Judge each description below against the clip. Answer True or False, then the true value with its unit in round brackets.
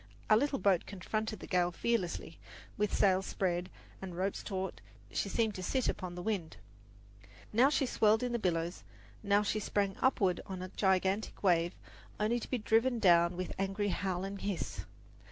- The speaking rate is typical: True (170 wpm)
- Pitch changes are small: False (3.0 semitones)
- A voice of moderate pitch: False (195 Hz)